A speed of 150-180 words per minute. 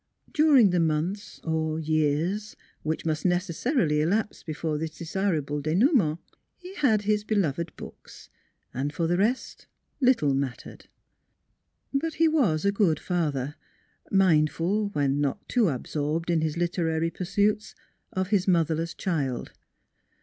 No: slow, 135 wpm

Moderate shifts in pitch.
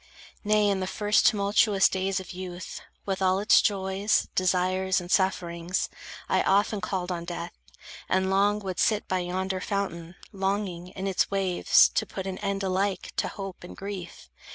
No: narrow, 1.4 semitones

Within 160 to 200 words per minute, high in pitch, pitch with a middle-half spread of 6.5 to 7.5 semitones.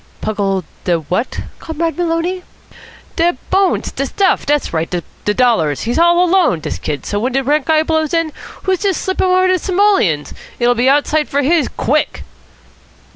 Yes: average, 175 wpm; very high, 305 Hz; wide, 7.2 semitones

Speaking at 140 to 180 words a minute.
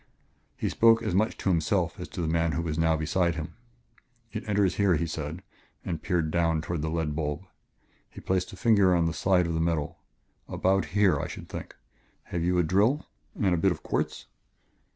No: fast, 205 wpm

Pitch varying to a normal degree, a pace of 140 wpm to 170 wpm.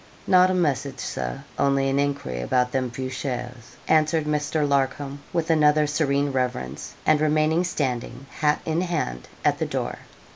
Yes: average, 3.1 semitones; average, 155 wpm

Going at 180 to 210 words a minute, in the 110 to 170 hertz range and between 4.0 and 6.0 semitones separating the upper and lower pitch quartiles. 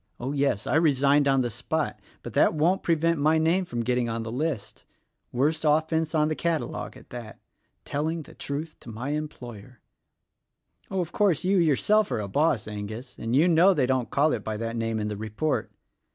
Yes: average, 200 wpm; medium, 140 Hz; average, 5.3 semitones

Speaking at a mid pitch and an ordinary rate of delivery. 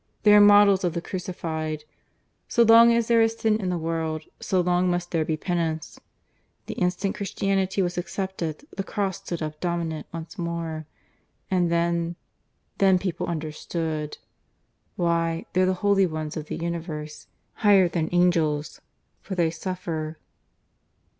Yes: medium, 175 Hz; average, 145 wpm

